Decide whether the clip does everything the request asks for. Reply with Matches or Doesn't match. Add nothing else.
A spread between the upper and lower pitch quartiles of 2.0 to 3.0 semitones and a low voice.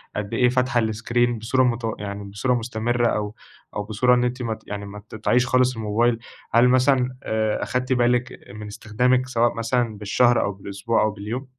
Matches